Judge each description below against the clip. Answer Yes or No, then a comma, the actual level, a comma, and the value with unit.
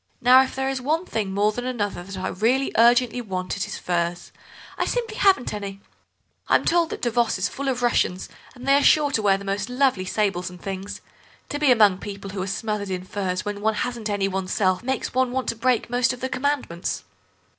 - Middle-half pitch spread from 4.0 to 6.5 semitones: Yes, average, 4.7 semitones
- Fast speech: Yes, fast, 220 wpm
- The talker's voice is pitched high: Yes, high, 220 Hz